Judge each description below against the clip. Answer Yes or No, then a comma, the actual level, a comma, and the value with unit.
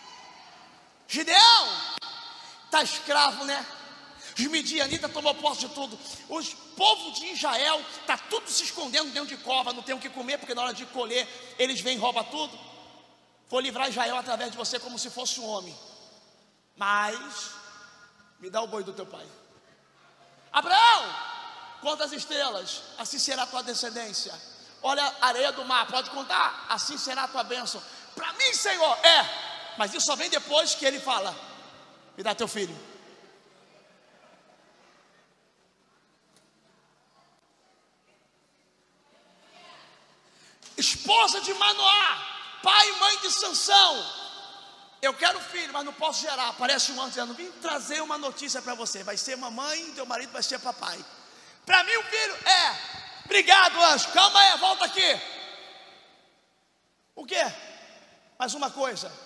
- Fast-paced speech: No, average, 145 wpm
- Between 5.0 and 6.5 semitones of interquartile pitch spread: Yes, wide, 5.5 semitones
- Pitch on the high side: Yes, very high, 280 Hz